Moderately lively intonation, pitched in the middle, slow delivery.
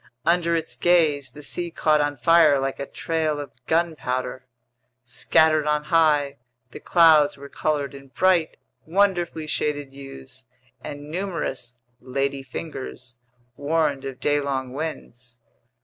Yes: average, 3.0 semitones; medium, 145 Hz; slow, 120 wpm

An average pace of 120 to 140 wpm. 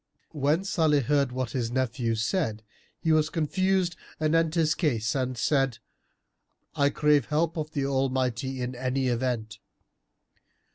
Yes: slow, 135 wpm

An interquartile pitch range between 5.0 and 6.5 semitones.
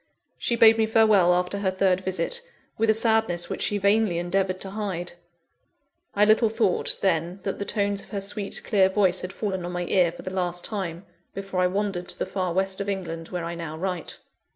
No: narrow, 2.5 semitones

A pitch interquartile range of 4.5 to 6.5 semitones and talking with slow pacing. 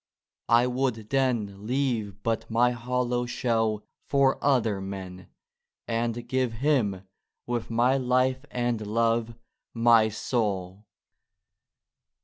No: average, 2.7 semitones; slow, 110 wpm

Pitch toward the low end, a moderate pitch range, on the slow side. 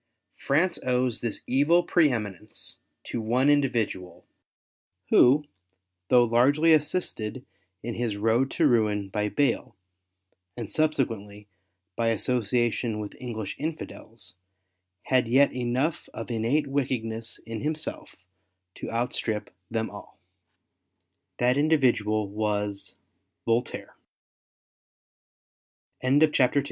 Yes: low, 120 Hz; average, 4.2 semitones; slow, 90 wpm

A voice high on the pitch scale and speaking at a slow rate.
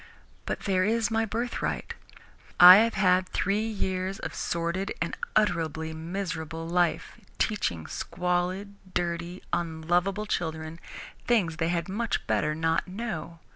No: medium, 180 Hz; slow, 125 wpm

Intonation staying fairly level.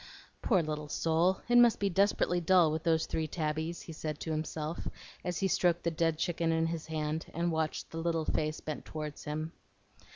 Yes: narrow, 1.8 semitones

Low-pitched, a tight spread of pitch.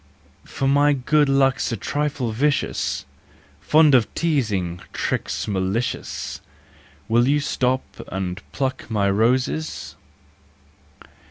No: low, 130 Hz; average, 4.8 semitones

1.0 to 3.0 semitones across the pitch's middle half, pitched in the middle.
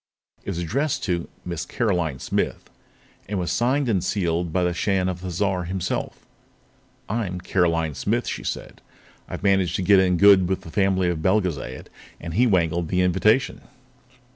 No: narrow, 2.4 semitones; very low, 90 Hz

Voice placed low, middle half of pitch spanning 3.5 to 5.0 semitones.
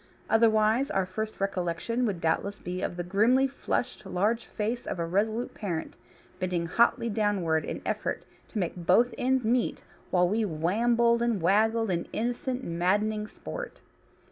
No: high, 210 Hz; average, 4.4 semitones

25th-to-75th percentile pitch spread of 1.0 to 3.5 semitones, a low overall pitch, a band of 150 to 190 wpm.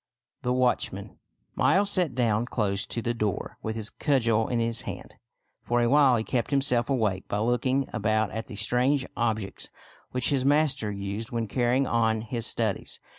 Yes: average, 2.8 semitones; low, 120 Hz; average, 175 wpm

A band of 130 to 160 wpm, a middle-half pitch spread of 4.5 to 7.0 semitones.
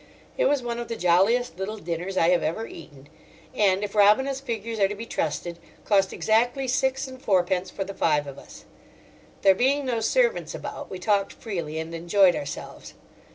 No: average, 185 wpm; average, 5.2 semitones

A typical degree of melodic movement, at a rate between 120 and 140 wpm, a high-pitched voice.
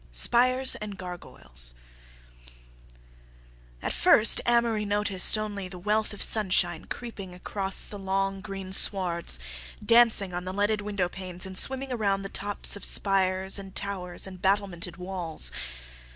No: narrow, 2.3 semitones; slow, 135 wpm; high, 195 Hz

